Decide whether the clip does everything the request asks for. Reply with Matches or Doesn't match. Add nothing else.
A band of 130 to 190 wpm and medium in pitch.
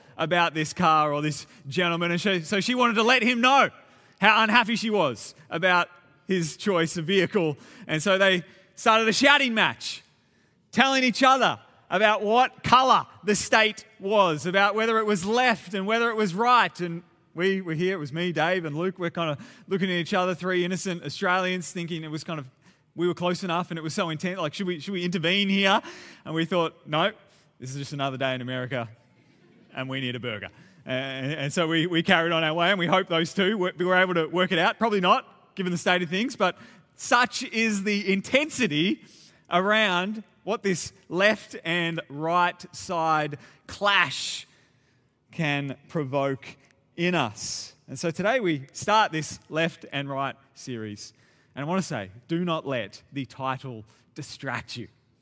Matches